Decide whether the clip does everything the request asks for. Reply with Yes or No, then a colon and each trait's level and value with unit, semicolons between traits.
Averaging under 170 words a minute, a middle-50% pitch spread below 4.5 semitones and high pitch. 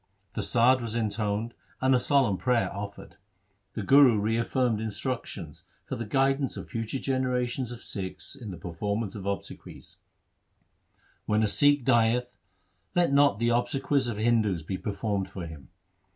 No: average, 160 wpm; average, 3.8 semitones; low, 115 Hz